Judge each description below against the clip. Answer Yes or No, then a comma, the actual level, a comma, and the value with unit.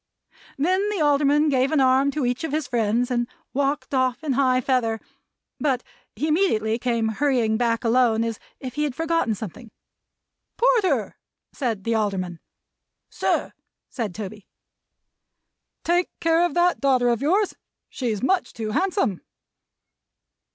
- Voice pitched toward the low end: No, very high, 255 Hz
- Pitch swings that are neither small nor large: Yes, average, 4.8 semitones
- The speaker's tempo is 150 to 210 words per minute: No, average, 140 wpm